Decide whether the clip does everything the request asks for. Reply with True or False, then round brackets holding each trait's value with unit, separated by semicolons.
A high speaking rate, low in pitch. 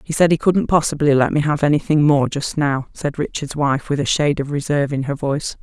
False (245 wpm; 145 Hz)